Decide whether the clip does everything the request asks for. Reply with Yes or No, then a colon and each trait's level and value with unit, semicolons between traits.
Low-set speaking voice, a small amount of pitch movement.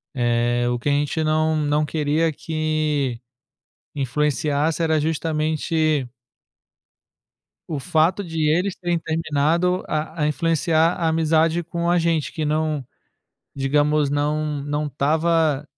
No: medium, 155 Hz; narrow, 1.9 semitones